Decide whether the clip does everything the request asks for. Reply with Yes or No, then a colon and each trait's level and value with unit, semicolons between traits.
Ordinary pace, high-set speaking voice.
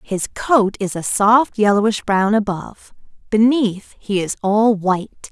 Yes: average, 145 wpm; high, 210 Hz